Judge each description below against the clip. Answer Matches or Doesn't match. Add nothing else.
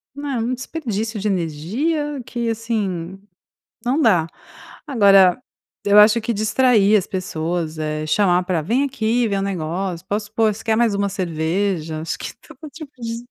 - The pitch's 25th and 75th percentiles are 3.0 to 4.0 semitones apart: Doesn't match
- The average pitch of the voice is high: Matches